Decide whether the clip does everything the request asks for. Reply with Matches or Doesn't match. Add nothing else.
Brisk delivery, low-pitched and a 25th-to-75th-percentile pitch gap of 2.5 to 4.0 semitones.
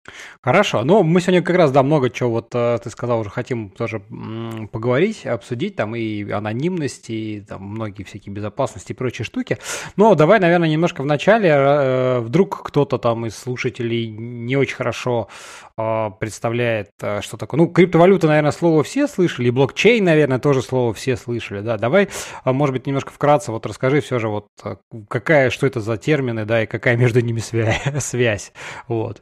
Doesn't match